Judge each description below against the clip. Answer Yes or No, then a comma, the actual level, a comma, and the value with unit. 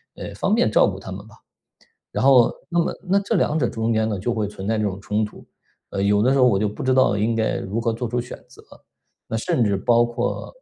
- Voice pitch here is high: No, low, 115 Hz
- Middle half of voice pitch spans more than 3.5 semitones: No, average, 3.1 semitones